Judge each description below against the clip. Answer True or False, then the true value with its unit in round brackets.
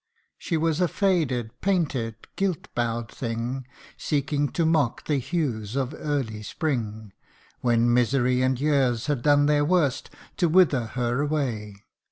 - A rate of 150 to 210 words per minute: False (140 wpm)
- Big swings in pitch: False (4.3 semitones)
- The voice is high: False (135 Hz)